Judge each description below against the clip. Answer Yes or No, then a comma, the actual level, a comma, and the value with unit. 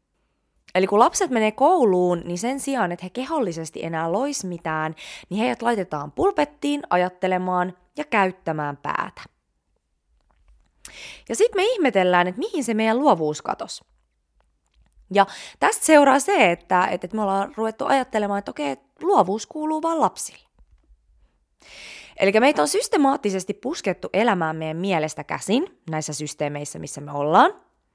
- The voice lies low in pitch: No, high, 195 Hz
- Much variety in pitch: Yes, wide, 8.7 semitones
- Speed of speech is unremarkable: Yes, average, 135 wpm